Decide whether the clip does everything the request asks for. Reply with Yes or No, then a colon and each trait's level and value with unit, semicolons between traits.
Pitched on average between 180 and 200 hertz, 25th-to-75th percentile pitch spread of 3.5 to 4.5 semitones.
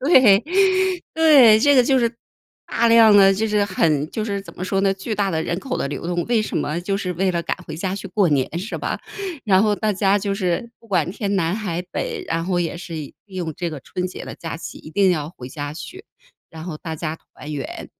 Yes: high, 190 Hz; average, 4.2 semitones